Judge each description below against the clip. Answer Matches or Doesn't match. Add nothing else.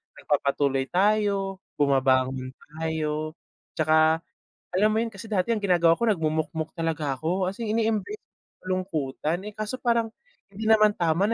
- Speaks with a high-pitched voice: Doesn't match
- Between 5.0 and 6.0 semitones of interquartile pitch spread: Matches